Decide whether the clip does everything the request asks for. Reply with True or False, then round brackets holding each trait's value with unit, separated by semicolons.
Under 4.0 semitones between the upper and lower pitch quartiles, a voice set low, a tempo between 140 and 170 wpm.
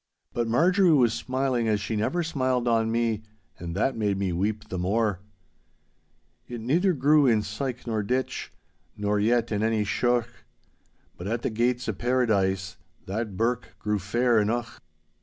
True (3.0 semitones; 115 Hz; 160 wpm)